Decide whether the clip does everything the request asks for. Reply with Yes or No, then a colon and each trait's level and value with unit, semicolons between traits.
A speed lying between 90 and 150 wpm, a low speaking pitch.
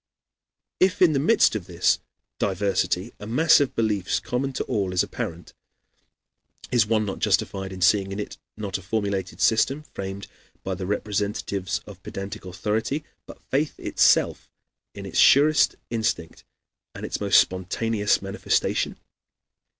Yes: average, 140 wpm; low, 105 Hz